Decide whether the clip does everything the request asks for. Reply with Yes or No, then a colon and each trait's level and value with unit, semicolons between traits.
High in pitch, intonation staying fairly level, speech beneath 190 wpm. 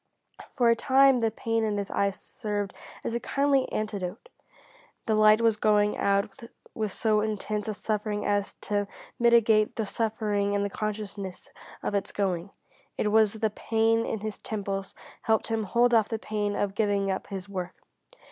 Yes: high, 215 Hz; narrow, 1.8 semitones; average, 170 wpm